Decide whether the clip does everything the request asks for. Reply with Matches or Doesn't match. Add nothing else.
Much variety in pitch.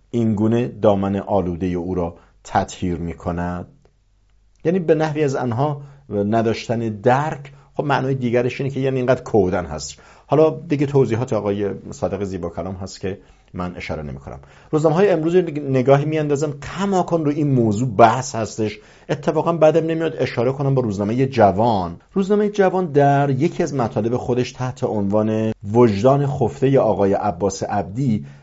Matches